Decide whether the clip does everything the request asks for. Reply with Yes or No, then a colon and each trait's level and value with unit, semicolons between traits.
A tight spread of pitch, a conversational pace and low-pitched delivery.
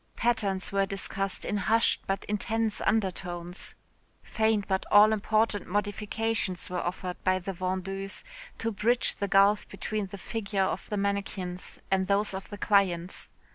No: narrow, 2.0 semitones; average, 145 wpm; high, 200 Hz